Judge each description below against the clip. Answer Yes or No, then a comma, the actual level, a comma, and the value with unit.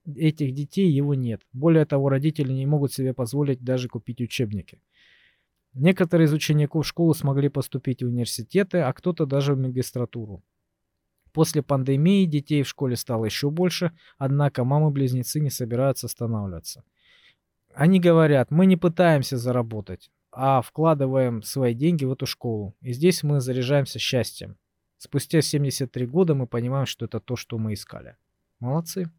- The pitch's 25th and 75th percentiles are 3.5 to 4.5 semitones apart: Yes, average, 3.9 semitones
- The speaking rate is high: No, average, 145 wpm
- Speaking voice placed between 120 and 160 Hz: Yes, low, 135 Hz